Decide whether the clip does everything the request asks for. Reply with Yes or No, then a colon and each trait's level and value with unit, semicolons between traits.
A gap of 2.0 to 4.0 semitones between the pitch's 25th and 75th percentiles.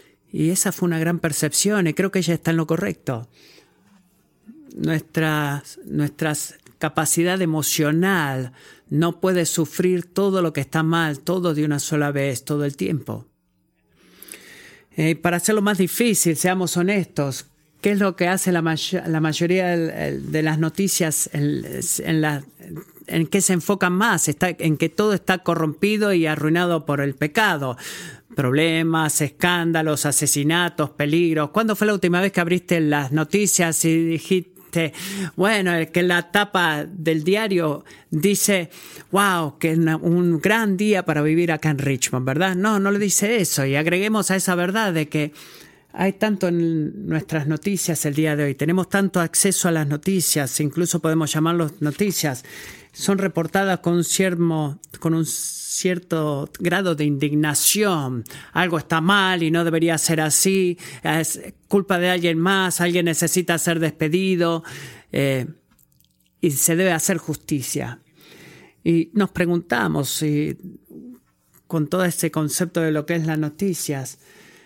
Yes: average, 3.1 semitones